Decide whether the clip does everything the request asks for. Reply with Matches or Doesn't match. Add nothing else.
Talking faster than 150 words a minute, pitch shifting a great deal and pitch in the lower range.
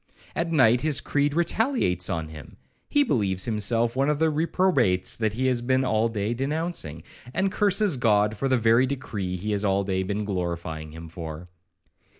Matches